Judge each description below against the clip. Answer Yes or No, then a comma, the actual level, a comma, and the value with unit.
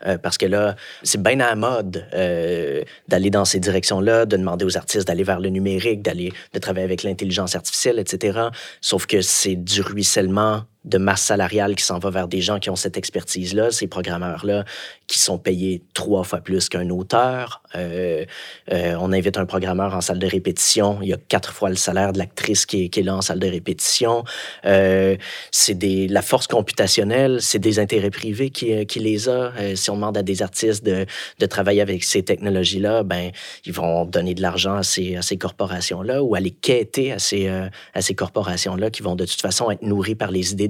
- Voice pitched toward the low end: Yes, very low, 95 Hz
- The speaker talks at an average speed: Yes, average, 210 wpm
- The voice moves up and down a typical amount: No, narrow, 1.8 semitones